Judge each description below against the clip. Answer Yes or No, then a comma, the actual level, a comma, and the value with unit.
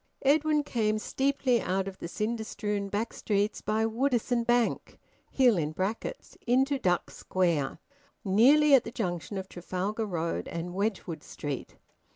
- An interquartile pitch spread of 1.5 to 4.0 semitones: No, average, 4.7 semitones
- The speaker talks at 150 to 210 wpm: No, slow, 135 wpm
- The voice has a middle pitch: No, high, 215 Hz